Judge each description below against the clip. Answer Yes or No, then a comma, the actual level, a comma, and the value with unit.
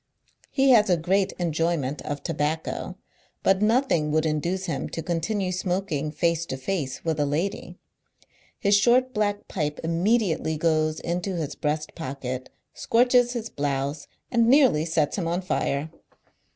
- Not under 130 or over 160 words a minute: Yes, average, 145 wpm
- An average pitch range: Yes, average, 4.8 semitones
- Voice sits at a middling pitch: Yes, medium, 170 Hz